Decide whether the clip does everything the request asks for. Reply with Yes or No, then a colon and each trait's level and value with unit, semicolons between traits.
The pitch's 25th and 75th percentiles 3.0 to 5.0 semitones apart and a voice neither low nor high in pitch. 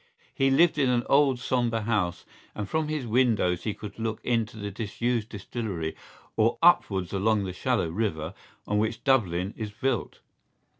No: average, 3.9 semitones; low, 110 Hz